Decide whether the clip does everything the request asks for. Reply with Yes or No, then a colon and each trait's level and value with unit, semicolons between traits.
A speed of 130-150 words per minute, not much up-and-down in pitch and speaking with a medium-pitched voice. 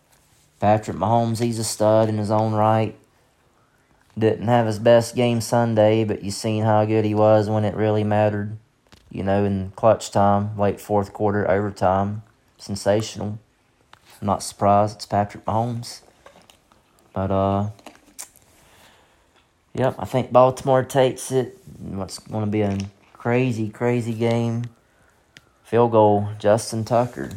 No: slow, 135 wpm; narrow, 2.3 semitones; low, 110 Hz